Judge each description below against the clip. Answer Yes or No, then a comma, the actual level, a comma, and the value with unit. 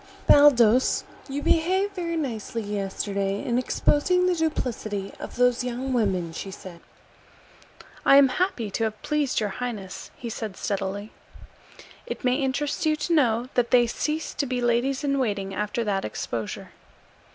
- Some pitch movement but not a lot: No, wide, 5.7 semitones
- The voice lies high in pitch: Yes, high, 245 Hz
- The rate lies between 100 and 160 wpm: Yes, average, 150 wpm